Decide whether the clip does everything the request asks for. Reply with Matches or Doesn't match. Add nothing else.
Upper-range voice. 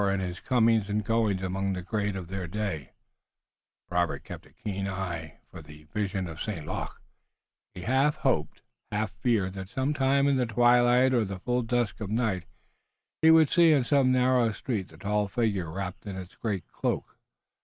Doesn't match